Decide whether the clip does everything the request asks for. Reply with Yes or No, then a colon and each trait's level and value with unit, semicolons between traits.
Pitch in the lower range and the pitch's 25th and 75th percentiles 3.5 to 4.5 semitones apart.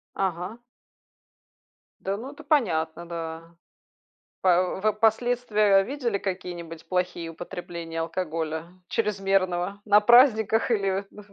No: high, 190 Hz; average, 3.9 semitones